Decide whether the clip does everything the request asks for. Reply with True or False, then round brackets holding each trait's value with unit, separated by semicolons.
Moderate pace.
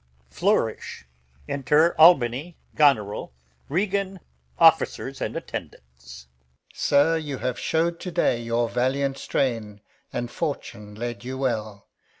False (105 wpm)